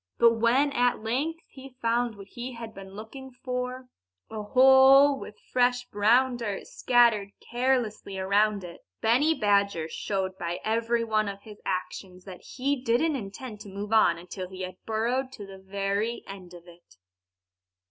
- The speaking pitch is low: No, high, 220 Hz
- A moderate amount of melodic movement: Yes, average, 4.2 semitones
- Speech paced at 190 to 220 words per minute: No, average, 160 wpm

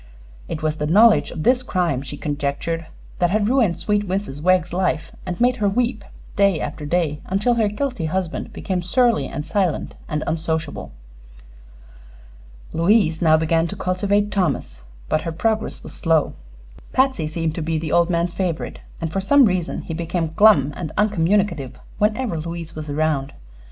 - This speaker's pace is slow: No, average, 165 wpm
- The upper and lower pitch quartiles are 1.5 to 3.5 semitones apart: No, average, 4.4 semitones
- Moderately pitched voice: Yes, medium, 170 Hz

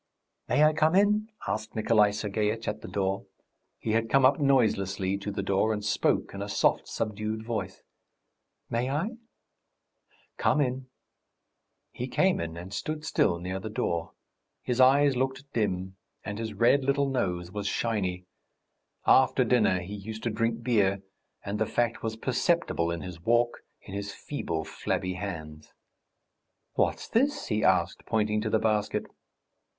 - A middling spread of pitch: Yes, average, 4.5 semitones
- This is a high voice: No, low, 110 Hz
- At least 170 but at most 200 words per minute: No, average, 155 wpm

